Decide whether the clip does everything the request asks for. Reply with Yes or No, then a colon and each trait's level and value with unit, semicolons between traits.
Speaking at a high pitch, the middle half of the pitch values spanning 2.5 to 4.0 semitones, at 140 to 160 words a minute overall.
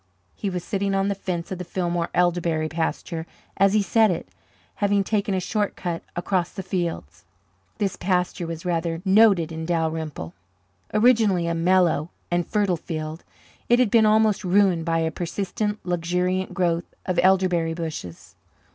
No: medium, 180 Hz; average, 3.0 semitones; average, 155 wpm